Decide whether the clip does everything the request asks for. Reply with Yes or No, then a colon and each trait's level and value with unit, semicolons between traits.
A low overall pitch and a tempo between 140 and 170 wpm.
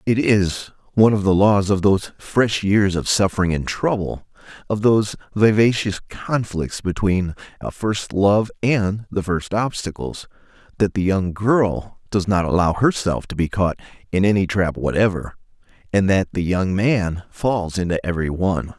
Yes: low, 100 Hz; average, 160 wpm